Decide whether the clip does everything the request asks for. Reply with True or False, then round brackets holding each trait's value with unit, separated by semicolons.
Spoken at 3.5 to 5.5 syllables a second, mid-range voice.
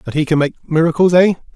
False (6.1 syllables/s; 160 Hz)